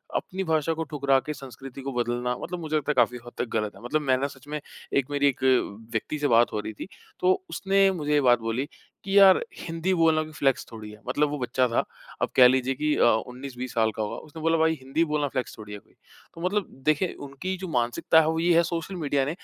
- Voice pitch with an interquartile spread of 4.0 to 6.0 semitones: Yes, average, 4.6 semitones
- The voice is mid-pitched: Yes, medium, 145 Hz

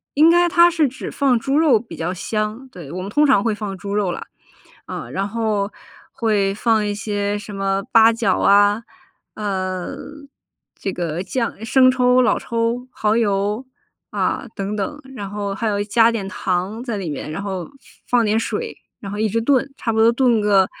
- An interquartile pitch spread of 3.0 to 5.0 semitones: Yes, average, 3.3 semitones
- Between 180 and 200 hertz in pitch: No, high, 215 Hz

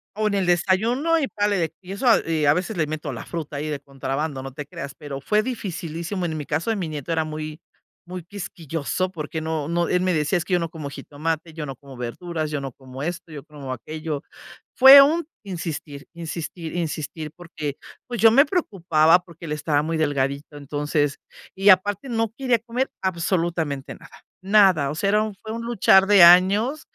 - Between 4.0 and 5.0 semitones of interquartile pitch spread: Yes, average, 4.5 semitones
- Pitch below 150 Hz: No, medium, 165 Hz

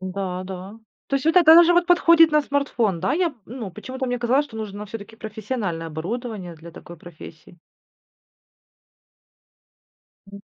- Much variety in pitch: Yes, wide, 7.0 semitones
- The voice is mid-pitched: No, high, 220 Hz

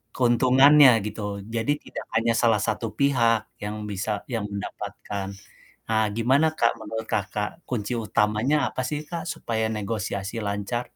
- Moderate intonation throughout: Yes, average, 3.1 semitones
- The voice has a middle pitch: No, low, 115 Hz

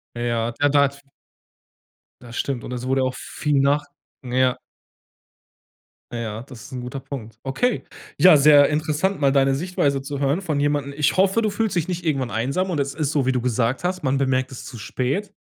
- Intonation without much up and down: No, average, 3.1 semitones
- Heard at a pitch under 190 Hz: Yes, medium, 140 Hz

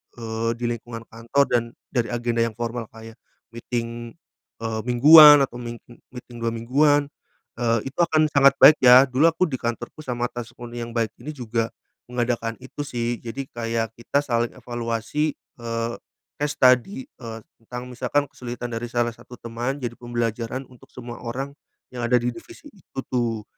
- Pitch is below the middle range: Yes, low, 120 Hz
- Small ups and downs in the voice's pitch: Yes, narrow, 2.2 semitones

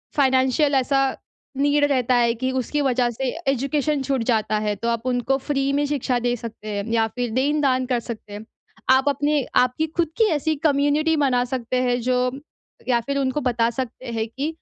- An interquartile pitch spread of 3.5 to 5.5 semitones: No, average, 2.9 semitones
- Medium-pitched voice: No, very high, 255 Hz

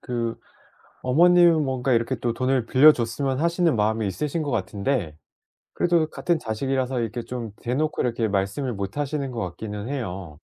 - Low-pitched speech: Yes, low, 125 Hz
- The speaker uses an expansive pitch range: No, average, 4.5 semitones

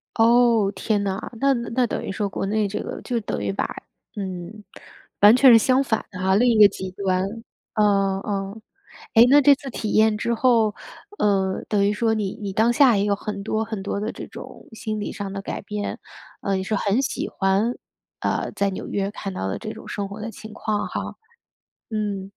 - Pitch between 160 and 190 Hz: No, high, 210 Hz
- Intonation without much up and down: Yes, narrow, 2.3 semitones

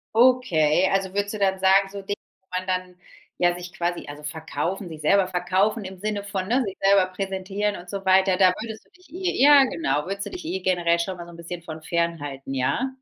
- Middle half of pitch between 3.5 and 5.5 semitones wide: No, average, 2.8 semitones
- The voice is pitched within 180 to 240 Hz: Yes, high, 190 Hz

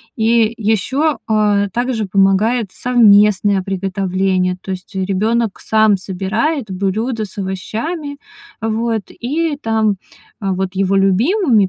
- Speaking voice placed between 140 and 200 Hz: No, high, 210 Hz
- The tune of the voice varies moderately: Yes, average, 3.3 semitones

